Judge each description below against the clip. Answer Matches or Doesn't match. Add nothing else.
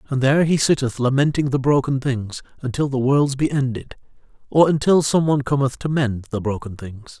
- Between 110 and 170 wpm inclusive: Doesn't match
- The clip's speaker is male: Matches